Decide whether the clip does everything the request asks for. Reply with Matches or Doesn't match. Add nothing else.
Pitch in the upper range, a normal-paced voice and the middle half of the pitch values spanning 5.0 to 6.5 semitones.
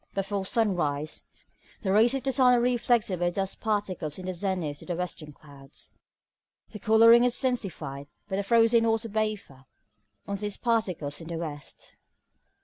Matches